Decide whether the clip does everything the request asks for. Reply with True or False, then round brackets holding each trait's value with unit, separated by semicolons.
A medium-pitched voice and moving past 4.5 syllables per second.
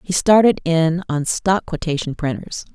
False (165 Hz; 4.4 syllables/s)